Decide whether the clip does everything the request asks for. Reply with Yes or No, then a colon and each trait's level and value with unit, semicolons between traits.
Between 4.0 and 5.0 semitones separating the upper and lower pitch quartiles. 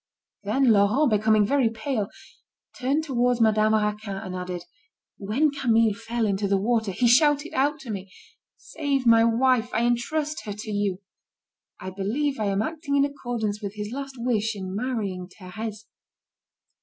Yes: average, 4.3 semitones